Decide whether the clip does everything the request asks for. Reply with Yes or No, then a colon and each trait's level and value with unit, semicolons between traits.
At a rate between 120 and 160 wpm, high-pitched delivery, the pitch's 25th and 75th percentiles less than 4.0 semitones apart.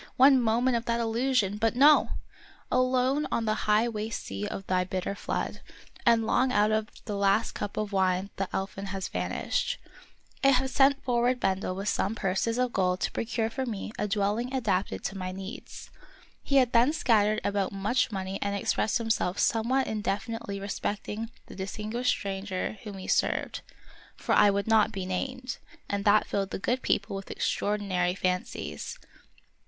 No: average, 175 wpm; high, 210 Hz; average, 3.4 semitones